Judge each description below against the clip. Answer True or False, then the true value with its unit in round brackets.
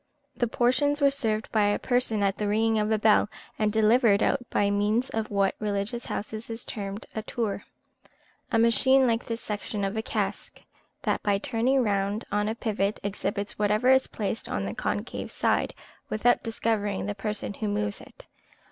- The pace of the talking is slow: False (185 wpm)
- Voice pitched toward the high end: True (215 Hz)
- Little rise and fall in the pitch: True (2.2 semitones)